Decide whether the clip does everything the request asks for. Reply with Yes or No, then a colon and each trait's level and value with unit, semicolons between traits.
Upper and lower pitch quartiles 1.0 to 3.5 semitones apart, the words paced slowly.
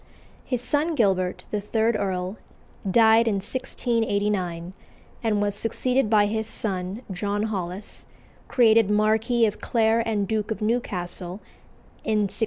Yes: narrow, 2.5 semitones; slow, 130 wpm